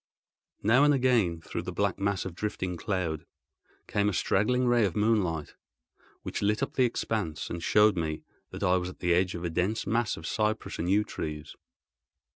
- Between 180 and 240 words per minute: Yes, average, 190 wpm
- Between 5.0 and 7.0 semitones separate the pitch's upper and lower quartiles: No, average, 4.1 semitones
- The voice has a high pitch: No, low, 100 Hz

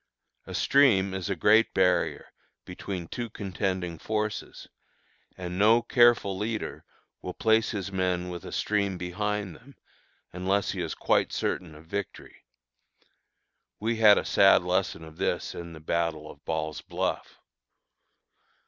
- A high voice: No, very low, 95 Hz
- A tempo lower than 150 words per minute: Yes, average, 140 wpm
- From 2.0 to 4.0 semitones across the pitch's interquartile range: Yes, average, 3.4 semitones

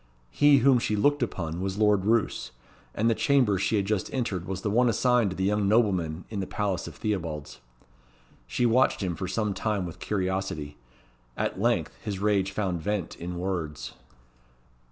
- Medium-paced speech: Yes, average, 175 wpm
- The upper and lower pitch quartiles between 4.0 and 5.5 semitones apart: No, average, 3.2 semitones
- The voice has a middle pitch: No, low, 100 Hz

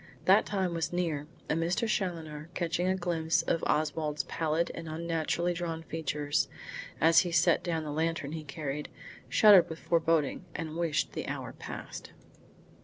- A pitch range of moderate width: No, narrow, 1.9 semitones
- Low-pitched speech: No, medium, 165 Hz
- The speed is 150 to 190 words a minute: Yes, average, 155 wpm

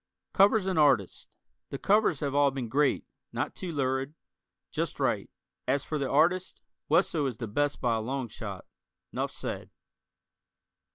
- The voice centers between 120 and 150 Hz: Yes, medium, 140 Hz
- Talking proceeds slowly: No, average, 155 wpm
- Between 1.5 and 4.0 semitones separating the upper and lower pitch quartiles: Yes, average, 3.7 semitones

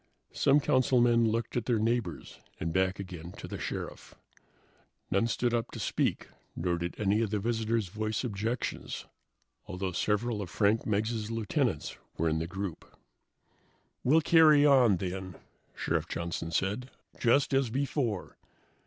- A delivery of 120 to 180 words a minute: Yes, average, 145 wpm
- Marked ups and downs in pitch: No, average, 4.2 semitones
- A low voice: Yes, low, 110 Hz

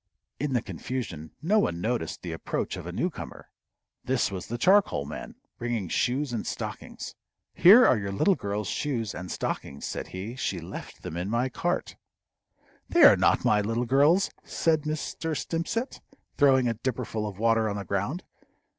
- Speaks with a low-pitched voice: Yes, low, 120 Hz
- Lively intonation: Yes, wide, 6.2 semitones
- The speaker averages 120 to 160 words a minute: No, average, 170 wpm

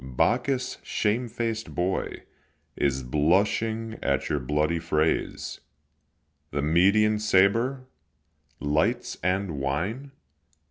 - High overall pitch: No, very low, 95 Hz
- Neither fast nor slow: No, slow, 85 wpm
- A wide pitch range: Yes, wide, 7.1 semitones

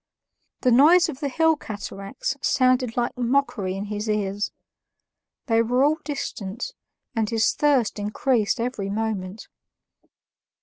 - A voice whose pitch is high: Yes, high, 230 Hz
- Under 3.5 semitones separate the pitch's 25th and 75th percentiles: No, average, 4.4 semitones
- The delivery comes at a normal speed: No, slow, 125 wpm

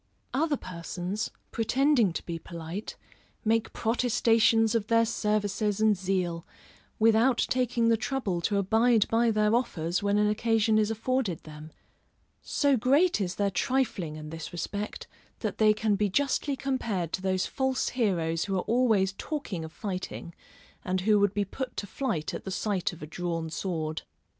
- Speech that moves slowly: No, average, 160 wpm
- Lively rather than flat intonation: No, average, 4.2 semitones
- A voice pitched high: Yes, high, 210 Hz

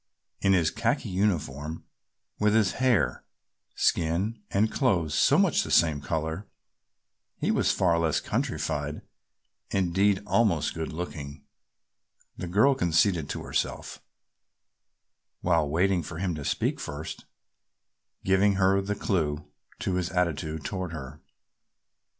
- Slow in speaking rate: Yes, slow, 120 wpm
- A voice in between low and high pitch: No, very low, 90 Hz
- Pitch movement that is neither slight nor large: Yes, average, 3.8 semitones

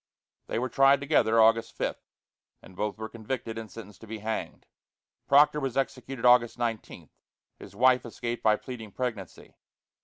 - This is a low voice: Yes, low, 115 Hz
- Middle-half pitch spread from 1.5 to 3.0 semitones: Yes, narrow, 2.6 semitones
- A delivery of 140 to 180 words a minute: Yes, average, 155 wpm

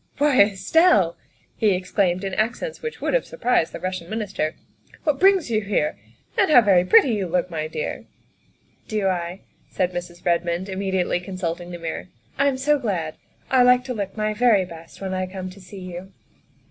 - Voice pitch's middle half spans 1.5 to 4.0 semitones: No, average, 5.1 semitones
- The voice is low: No, high, 190 Hz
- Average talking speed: No, fast, 210 wpm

